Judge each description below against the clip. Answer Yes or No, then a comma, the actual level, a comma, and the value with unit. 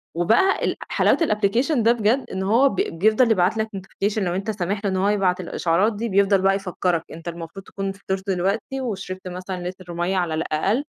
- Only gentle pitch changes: No, average, 3.1 semitones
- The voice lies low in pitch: No, high, 195 Hz